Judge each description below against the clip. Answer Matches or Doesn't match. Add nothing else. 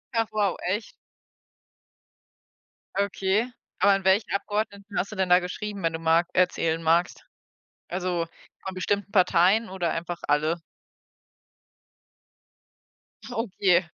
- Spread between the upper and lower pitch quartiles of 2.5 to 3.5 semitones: Matches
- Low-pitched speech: Doesn't match